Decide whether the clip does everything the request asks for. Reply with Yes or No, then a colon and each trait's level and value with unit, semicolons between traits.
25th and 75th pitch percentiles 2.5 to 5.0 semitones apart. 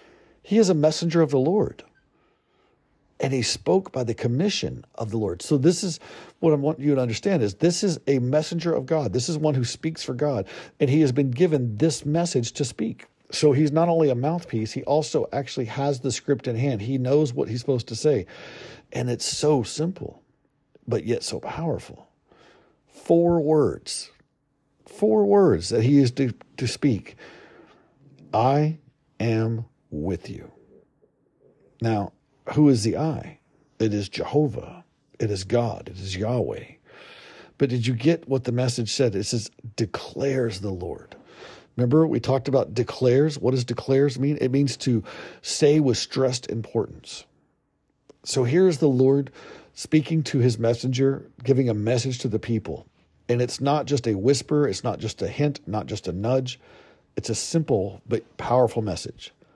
Yes: average, 4.2 semitones